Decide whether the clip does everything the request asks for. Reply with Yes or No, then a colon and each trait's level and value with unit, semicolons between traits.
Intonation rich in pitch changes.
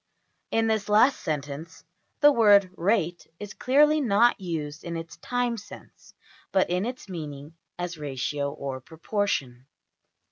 Yes: wide, 6.5 semitones